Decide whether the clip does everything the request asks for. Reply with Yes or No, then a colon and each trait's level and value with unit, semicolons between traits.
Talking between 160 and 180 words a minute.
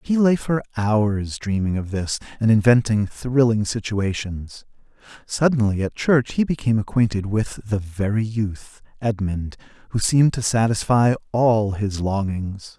No: slow, 135 wpm